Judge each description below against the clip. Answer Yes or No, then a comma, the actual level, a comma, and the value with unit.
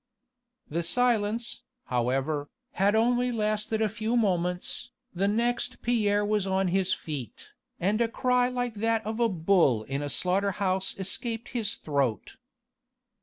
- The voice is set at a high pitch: Yes, high, 205 Hz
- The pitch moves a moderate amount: Yes, average, 4.4 semitones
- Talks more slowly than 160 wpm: Yes, average, 140 wpm